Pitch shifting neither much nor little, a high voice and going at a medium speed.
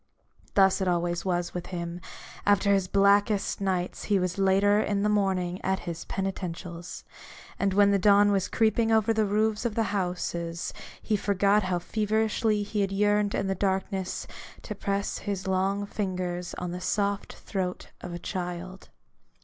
No: narrow, 2.2 semitones; high, 195 Hz; average, 165 wpm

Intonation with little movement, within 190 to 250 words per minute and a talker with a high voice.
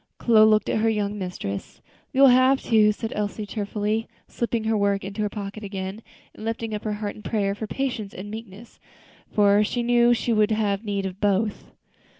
Yes: narrow, 1.8 semitones; average, 200 wpm; high, 215 Hz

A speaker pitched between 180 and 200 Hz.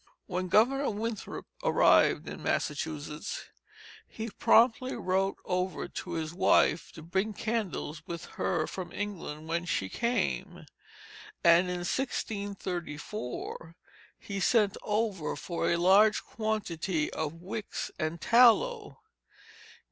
Yes: medium, 185 Hz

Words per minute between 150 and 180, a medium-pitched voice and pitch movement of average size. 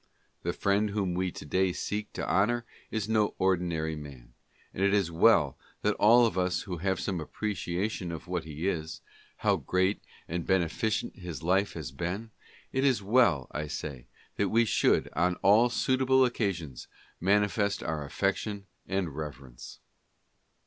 No: average, 165 wpm; very low, 95 Hz; average, 4.4 semitones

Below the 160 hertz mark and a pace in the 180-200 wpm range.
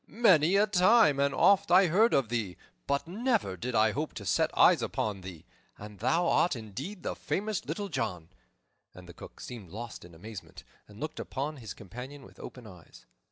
Yes: low, 135 Hz; average, 190 wpm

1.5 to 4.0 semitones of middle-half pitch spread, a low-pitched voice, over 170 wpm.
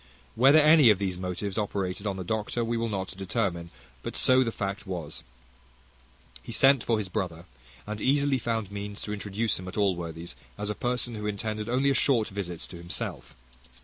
Yes: average, 3.7 semitones; low, 105 Hz; average, 185 wpm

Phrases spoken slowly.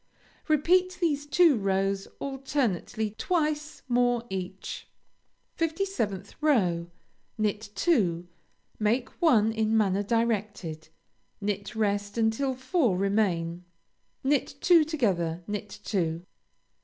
Yes: slow, 95 wpm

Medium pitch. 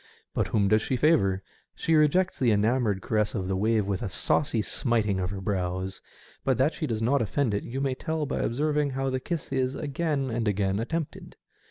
No: low, 115 Hz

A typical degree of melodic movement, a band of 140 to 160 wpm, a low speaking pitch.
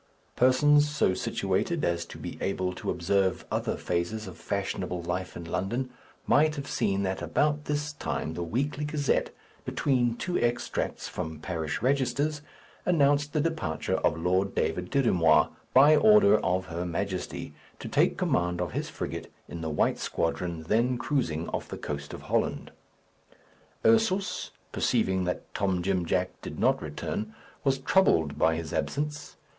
No: wide, 8.7 semitones; average, 155 wpm; low, 100 Hz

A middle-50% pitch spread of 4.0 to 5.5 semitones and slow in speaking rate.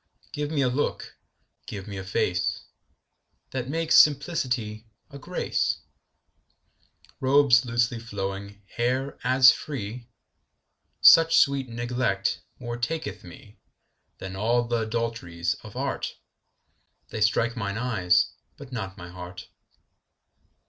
Yes: average, 4.5 semitones; slow, 115 wpm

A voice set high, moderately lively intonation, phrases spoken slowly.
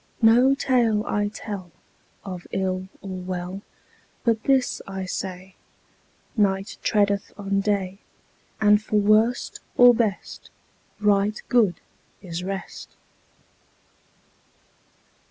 No: high, 200 Hz; narrow, 2.3 semitones; slow, 100 wpm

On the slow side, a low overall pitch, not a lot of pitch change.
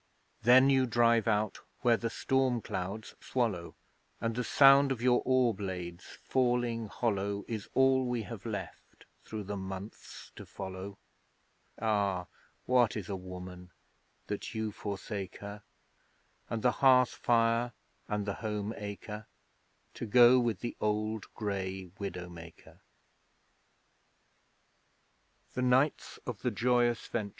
No: slow, 115 wpm; low, 110 Hz; average, 3.4 semitones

